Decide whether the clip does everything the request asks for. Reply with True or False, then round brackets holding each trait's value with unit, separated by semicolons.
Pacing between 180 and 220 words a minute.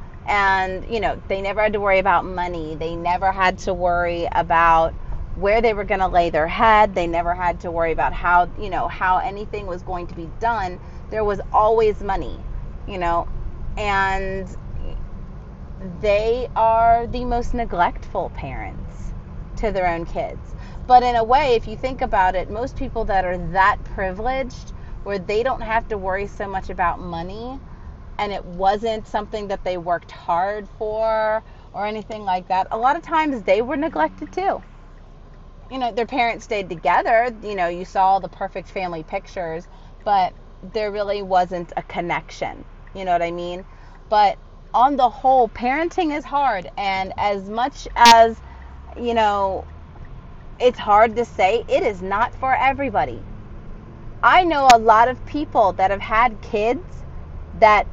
False (165 wpm)